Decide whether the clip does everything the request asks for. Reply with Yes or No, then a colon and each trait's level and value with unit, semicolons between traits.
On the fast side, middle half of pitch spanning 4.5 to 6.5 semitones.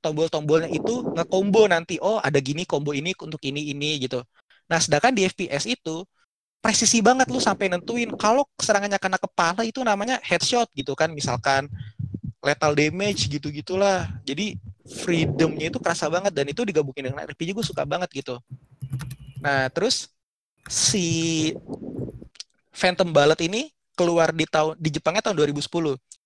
Yes: fast, 145 wpm; wide, 5.6 semitones